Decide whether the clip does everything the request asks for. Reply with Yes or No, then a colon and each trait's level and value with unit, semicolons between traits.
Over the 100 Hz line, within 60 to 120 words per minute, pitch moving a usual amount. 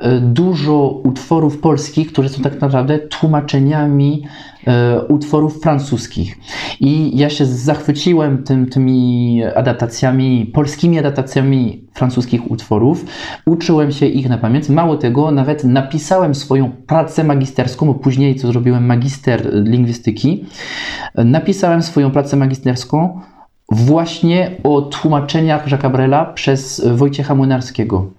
Yes: medium, 140 Hz; slow, 110 wpm; average, 3.1 semitones